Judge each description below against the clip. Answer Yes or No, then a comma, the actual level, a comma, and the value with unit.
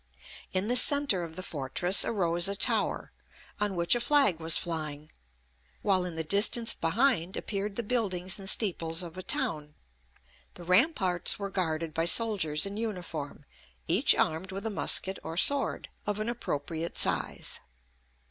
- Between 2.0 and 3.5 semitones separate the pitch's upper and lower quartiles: No, average, 4.2 semitones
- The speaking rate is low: No, average, 155 wpm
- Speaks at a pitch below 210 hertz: Yes, medium, 185 Hz